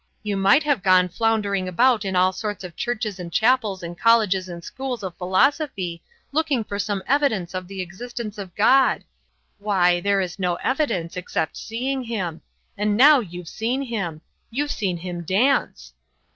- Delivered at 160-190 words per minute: Yes, average, 165 wpm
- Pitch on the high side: Yes, high, 200 Hz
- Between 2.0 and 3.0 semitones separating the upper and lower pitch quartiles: No, average, 4.8 semitones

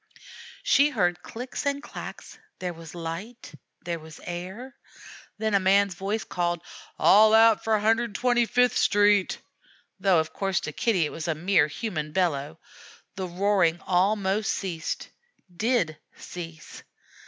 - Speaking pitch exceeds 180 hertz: Yes, high, 190 Hz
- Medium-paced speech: No, slow, 130 wpm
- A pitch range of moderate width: Yes, average, 4.3 semitones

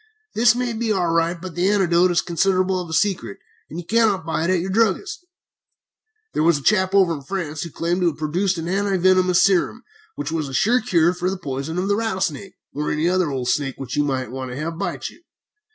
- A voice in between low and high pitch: Yes, medium, 175 Hz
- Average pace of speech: No, fast, 230 wpm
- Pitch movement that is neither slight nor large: Yes, average, 3.5 semitones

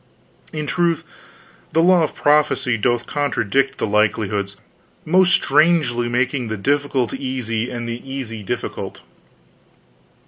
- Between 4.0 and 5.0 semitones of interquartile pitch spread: Yes, average, 4.5 semitones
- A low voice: Yes, low, 130 Hz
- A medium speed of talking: No, slow, 115 wpm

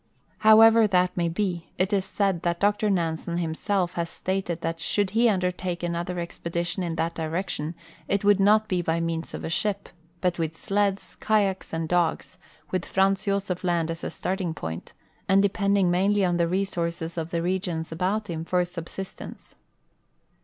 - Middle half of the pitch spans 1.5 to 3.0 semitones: Yes, average, 2.7 semitones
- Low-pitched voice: No, medium, 180 Hz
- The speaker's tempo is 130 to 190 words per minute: Yes, average, 175 wpm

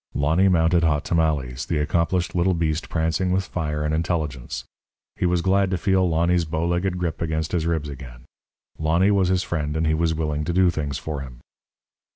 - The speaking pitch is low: Yes, very low, 80 Hz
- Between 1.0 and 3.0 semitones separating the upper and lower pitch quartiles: Yes, average, 2.7 semitones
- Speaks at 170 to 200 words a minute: Yes, average, 190 wpm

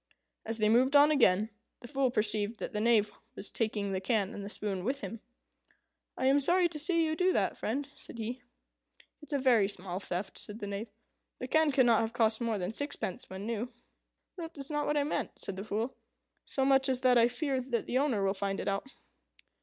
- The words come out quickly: Yes, fast, 215 wpm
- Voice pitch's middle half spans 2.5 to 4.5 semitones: No, average, 4.9 semitones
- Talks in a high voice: Yes, high, 235 Hz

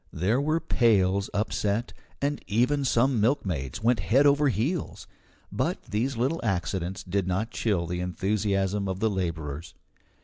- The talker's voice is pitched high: No, low, 105 Hz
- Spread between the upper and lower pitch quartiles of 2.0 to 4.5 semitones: No, average, 5.0 semitones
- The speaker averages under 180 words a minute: Yes, average, 140 wpm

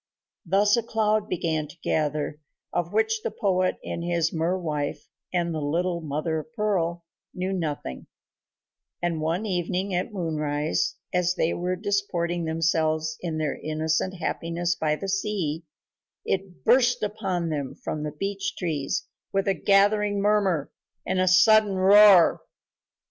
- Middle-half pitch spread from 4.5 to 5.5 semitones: No, average, 3.7 semitones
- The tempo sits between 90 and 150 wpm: Yes, average, 140 wpm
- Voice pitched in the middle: Yes, medium, 175 Hz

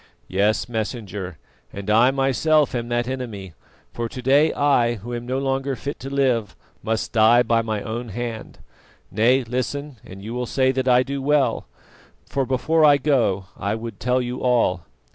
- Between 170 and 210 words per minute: Yes, average, 175 wpm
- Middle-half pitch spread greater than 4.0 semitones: No, average, 3.3 semitones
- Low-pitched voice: Yes, low, 120 Hz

